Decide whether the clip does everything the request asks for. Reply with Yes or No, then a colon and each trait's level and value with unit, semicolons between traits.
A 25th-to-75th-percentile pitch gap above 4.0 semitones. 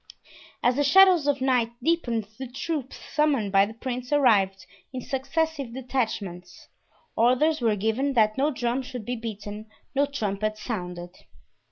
Yes: average, 4.6 semitones